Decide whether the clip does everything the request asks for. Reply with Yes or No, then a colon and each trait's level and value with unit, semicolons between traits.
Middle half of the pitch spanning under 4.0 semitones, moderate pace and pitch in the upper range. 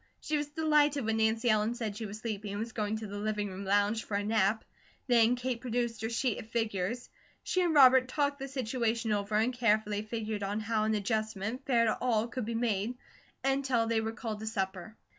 No: narrow, 2.6 semitones; fast, 215 wpm; high, 225 Hz